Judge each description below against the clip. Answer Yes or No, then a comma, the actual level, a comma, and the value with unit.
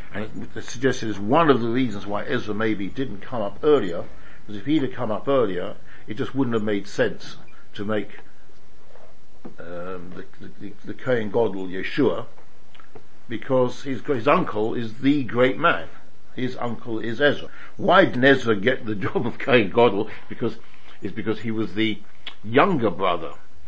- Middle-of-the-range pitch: No, low, 115 Hz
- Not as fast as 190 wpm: Yes, average, 165 wpm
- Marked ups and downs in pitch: No, average, 3.8 semitones